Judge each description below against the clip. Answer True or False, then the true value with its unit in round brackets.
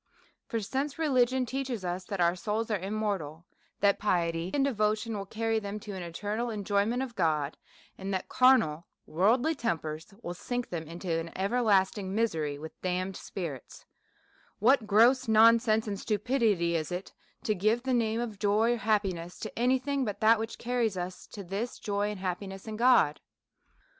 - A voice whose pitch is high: True (210 Hz)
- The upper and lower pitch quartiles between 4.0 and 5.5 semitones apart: True (4.3 semitones)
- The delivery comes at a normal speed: True (175 wpm)